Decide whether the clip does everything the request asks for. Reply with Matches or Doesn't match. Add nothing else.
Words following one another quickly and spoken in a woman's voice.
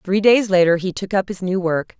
Matches